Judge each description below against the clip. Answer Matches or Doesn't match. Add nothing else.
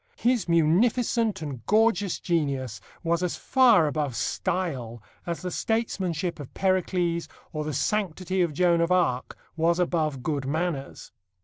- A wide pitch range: Doesn't match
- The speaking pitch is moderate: Matches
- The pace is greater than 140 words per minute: Doesn't match